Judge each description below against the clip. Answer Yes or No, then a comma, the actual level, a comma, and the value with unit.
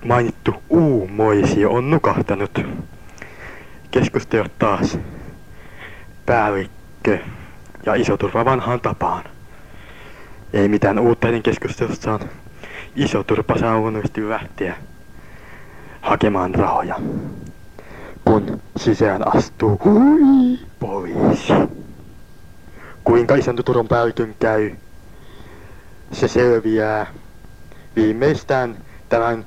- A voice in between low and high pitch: No, low, 115 Hz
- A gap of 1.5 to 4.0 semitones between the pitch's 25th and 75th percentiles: Yes, average, 2.8 semitones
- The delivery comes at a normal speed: No, slow, 75 wpm